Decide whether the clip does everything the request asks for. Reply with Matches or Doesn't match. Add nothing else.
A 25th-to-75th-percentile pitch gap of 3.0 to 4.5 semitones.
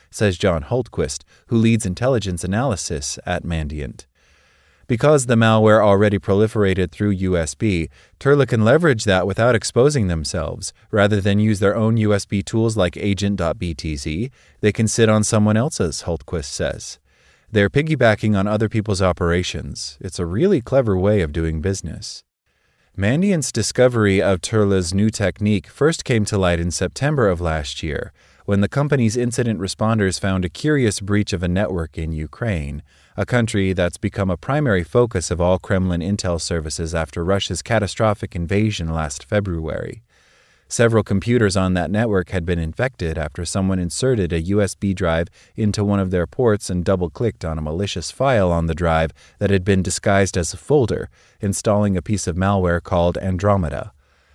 Matches